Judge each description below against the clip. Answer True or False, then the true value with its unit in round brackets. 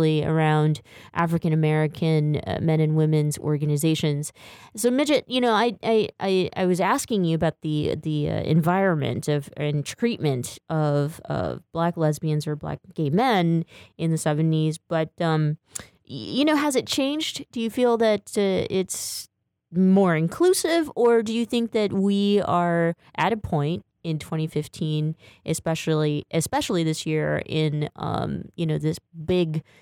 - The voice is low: False (160 Hz)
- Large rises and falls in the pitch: False (4.3 semitones)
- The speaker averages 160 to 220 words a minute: False (145 wpm)